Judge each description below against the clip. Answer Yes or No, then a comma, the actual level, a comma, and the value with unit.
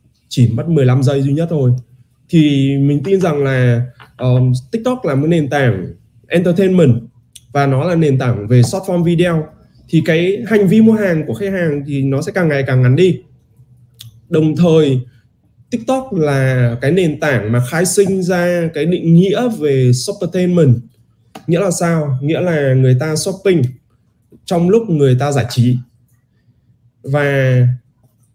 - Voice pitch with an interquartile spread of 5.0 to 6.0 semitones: Yes, wide, 5.6 semitones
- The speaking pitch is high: No, medium, 140 Hz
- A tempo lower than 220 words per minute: Yes, slow, 165 wpm